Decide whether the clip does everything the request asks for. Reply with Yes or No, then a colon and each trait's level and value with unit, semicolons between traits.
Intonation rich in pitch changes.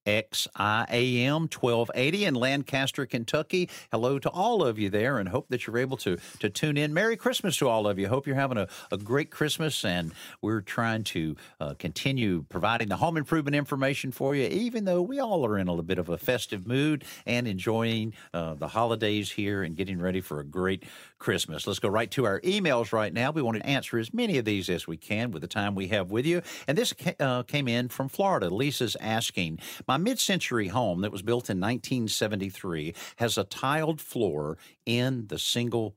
Yes: wide, 5.7 semitones